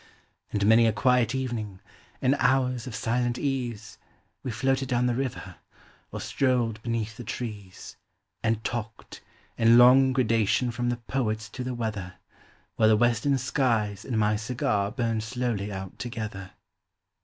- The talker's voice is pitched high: No, low, 115 Hz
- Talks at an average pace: Yes, average, 145 wpm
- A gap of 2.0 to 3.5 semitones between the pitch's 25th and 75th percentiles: Yes, average, 2.7 semitones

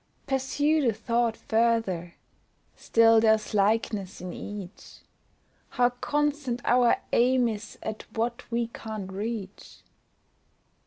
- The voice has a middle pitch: No, high, 230 Hz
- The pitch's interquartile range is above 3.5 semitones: No, average, 2.7 semitones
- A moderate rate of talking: No, slow, 105 wpm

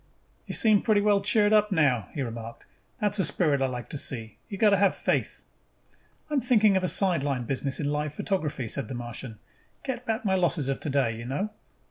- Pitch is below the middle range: No, medium, 155 Hz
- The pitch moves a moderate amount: No, wide, 7.8 semitones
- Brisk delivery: Yes, fast, 215 wpm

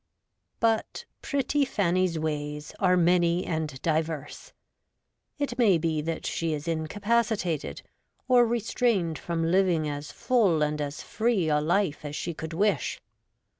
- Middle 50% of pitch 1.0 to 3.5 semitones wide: No, average, 4.9 semitones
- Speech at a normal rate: No, slow, 130 wpm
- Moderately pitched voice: Yes, medium, 170 Hz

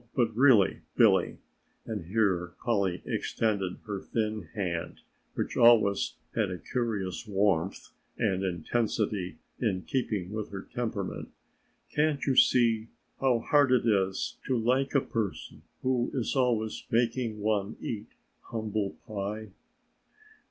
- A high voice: No, low, 110 Hz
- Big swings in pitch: No, average, 3.4 semitones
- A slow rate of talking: Yes, slow, 125 wpm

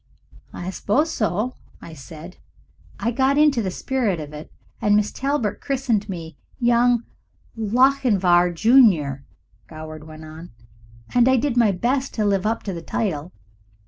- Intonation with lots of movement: Yes, wide, 6.3 semitones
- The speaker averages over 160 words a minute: No, average, 145 wpm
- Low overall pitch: No, high, 210 Hz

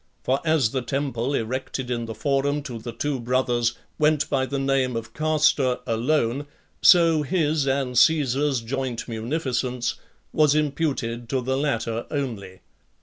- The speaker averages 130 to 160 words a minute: Yes, average, 145 wpm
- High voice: No, low, 135 Hz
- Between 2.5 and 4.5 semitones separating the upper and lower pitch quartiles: Yes, average, 3.6 semitones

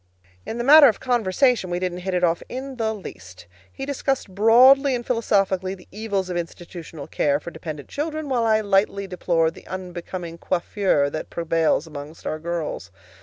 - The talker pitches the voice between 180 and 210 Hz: Yes, medium, 185 Hz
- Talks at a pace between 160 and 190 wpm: Yes, average, 170 wpm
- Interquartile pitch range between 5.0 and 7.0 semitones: Yes, wide, 5.5 semitones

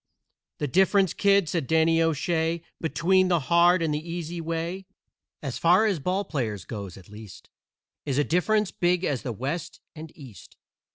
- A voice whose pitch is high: No, medium, 165 Hz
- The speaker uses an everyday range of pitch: Yes, average, 3.8 semitones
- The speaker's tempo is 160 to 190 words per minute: Yes, average, 165 wpm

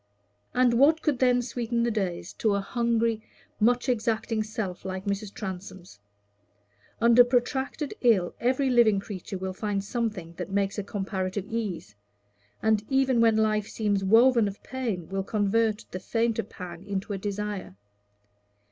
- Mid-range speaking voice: No, high, 215 Hz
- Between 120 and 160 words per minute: Yes, average, 145 wpm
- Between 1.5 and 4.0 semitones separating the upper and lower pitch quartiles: Yes, average, 3.3 semitones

